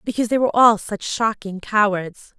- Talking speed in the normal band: Yes, average, 175 wpm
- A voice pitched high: Yes, high, 215 Hz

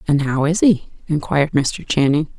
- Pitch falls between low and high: Yes, medium, 155 Hz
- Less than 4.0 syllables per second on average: No, 4.9 syllables/s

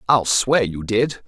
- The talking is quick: No, average, 190 wpm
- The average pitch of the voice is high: No, low, 115 Hz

